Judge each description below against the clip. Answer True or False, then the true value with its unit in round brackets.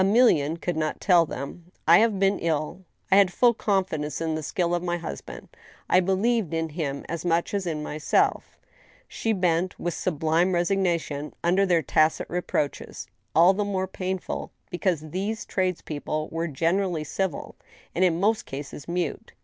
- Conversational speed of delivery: True (175 wpm)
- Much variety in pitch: False (3.2 semitones)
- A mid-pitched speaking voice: True (175 Hz)